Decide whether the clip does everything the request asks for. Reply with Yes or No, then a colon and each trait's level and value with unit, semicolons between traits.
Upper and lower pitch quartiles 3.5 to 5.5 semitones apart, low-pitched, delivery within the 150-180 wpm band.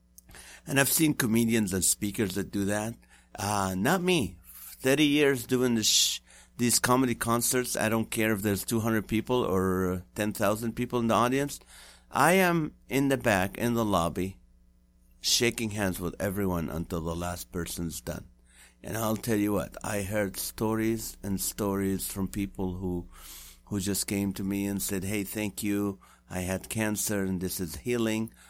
Yes: average, 3.9 semitones; low, 100 Hz; average, 170 wpm